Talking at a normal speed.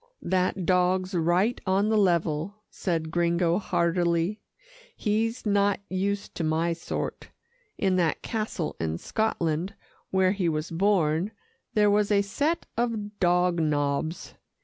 No: slow, 125 wpm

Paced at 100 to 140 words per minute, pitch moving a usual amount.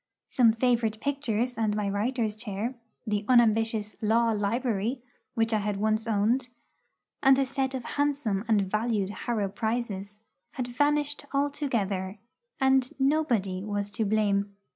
Yes: slow, 135 wpm; average, 3.7 semitones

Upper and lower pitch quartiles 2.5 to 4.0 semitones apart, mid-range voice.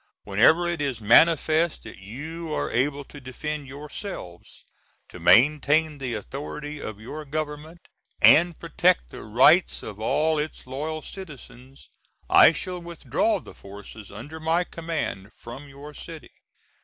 No: average, 4.6 semitones; medium, 150 Hz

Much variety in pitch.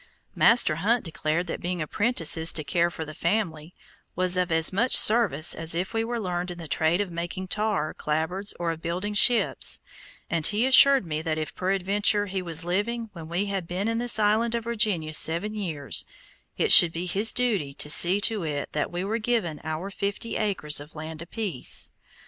No: average, 4.6 semitones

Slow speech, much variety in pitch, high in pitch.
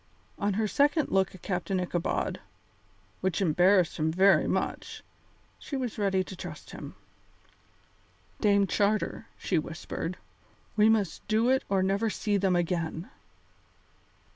No: slow, 130 wpm; average, 2.8 semitones; high, 195 Hz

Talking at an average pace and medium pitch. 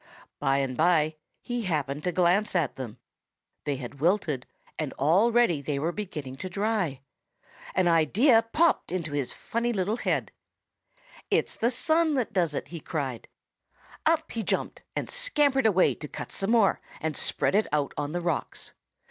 Yes: average, 165 wpm; medium, 175 Hz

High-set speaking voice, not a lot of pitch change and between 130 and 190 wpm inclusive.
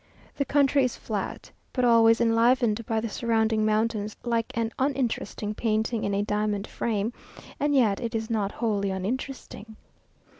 Yes: high, 225 Hz; narrow, 2.0 semitones; average, 150 wpm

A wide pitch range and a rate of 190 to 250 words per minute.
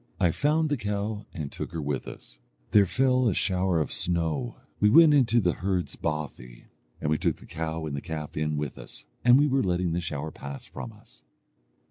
Yes: wide, 5.9 semitones; fast, 205 wpm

